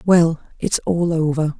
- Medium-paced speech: Yes, average, 150 wpm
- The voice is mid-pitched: Yes, medium, 165 Hz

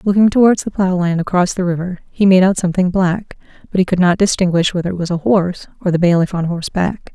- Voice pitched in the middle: Yes, medium, 180 Hz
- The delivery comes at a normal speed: No, fast, 235 wpm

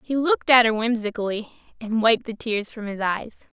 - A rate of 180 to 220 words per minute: Yes, average, 200 wpm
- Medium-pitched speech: No, high, 225 Hz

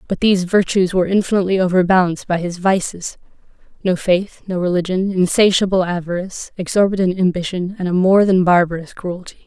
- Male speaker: No, female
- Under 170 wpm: Yes, average, 145 wpm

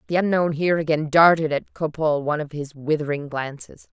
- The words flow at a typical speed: Yes, average, 180 wpm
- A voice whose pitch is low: No, medium, 155 Hz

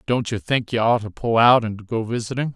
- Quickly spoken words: Yes, fast, 260 wpm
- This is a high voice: No, low, 115 Hz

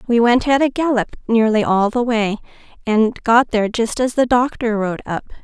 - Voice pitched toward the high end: Yes, high, 230 Hz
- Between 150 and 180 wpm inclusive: No, average, 190 wpm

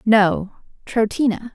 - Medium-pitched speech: No, high, 215 Hz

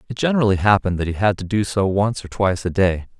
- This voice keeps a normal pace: No, fast, 265 wpm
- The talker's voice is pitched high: No, low, 100 Hz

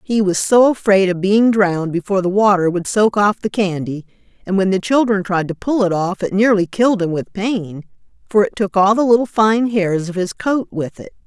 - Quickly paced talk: Yes, fast, 230 wpm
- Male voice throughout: No, female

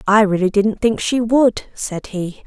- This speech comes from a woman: Yes, female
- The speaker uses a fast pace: No, average, 195 wpm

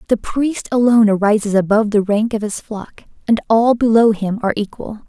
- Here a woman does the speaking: Yes, female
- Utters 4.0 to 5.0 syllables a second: No, 5.4 syllables/s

